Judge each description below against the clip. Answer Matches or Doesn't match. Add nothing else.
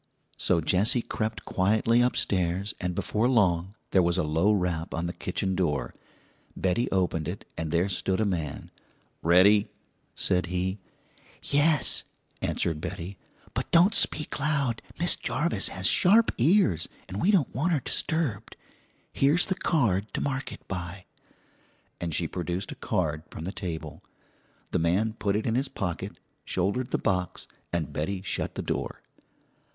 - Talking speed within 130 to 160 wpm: Matches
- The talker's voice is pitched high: Doesn't match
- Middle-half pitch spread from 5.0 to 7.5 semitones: Matches